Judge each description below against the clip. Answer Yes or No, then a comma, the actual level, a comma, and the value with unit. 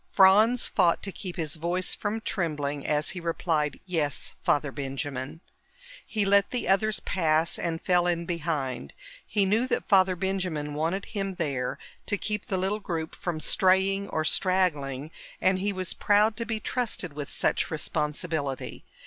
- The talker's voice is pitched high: No, medium, 175 Hz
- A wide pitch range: No, average, 4.4 semitones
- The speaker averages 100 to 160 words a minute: Yes, average, 155 wpm